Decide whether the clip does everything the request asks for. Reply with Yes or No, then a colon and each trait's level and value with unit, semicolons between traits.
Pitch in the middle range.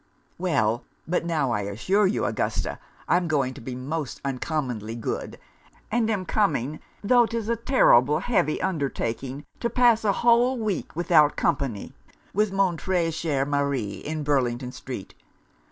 Yes: medium, 155 Hz